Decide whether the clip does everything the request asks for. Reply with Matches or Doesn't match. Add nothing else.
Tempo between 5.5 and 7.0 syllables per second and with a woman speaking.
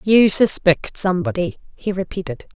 Doesn't match